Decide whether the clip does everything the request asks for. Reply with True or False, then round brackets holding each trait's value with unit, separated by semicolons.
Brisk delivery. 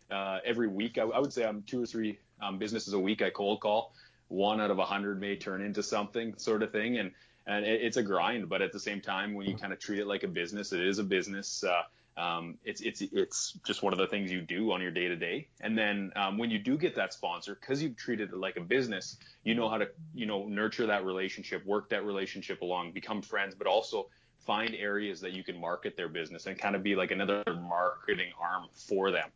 True (250 wpm)